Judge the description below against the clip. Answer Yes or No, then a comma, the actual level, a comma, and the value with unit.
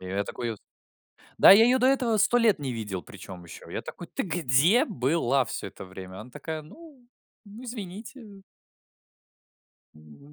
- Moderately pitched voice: Yes, medium, 160 Hz